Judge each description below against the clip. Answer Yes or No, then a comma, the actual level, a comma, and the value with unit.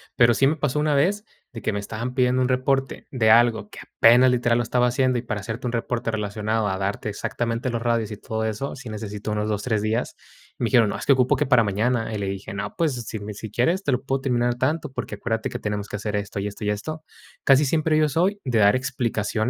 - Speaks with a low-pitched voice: Yes, low, 120 Hz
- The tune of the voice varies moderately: Yes, average, 3.5 semitones